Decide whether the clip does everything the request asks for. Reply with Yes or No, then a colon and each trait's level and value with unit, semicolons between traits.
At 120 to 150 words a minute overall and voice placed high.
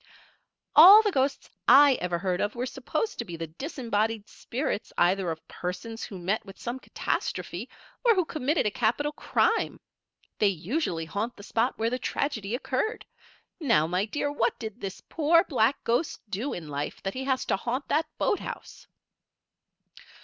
No: average, 165 wpm; high, 230 Hz